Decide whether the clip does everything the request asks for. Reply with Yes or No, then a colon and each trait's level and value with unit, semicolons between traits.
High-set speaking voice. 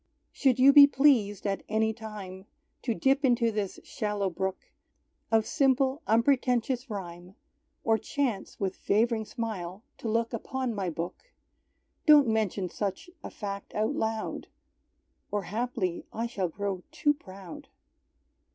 Yes: high, 220 Hz